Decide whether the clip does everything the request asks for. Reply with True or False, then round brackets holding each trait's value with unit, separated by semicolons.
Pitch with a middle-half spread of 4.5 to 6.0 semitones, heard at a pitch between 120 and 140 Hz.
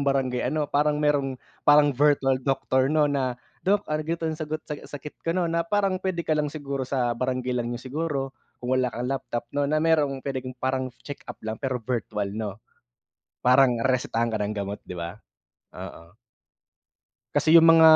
False (3.3 semitones; 135 Hz)